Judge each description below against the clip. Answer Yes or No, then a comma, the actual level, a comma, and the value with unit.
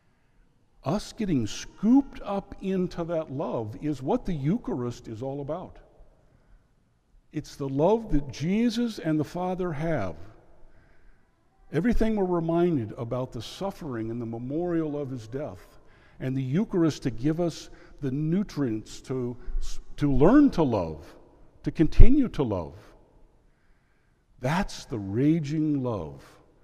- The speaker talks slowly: Yes, slow, 125 wpm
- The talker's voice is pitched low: No, medium, 150 Hz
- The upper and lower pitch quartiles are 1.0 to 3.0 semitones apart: No, wide, 5.6 semitones